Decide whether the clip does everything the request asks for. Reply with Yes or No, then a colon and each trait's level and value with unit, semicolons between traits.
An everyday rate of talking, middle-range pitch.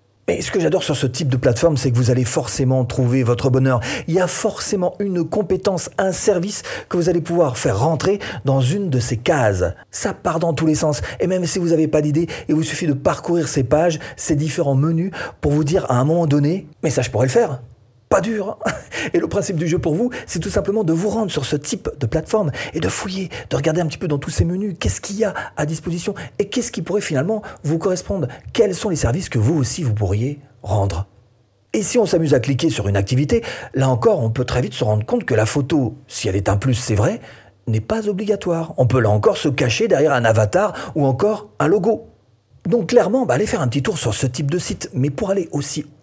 No: fast, 245 wpm; medium, 150 Hz